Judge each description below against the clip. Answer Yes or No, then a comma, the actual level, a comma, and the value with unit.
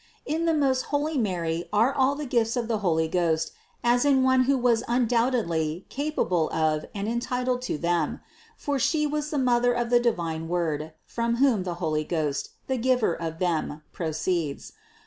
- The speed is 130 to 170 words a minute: No, average, 180 wpm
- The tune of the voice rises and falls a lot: Yes, wide, 7.6 semitones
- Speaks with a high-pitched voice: Yes, high, 230 Hz